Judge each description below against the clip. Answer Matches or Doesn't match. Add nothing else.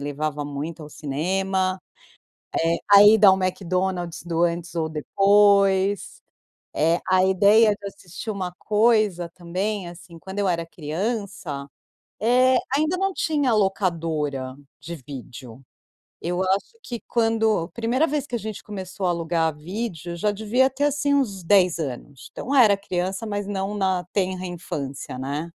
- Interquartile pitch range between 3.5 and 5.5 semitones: Matches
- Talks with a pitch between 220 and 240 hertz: Doesn't match